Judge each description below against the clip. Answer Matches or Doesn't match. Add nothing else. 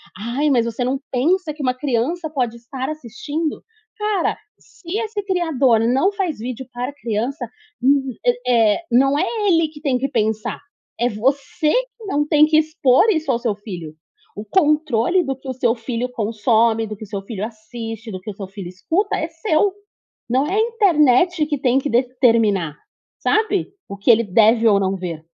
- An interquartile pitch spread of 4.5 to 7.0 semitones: Matches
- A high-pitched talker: Matches